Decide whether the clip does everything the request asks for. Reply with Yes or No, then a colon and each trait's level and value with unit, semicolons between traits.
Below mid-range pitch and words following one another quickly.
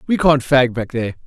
Yes: low, 130 Hz; fast, 235 wpm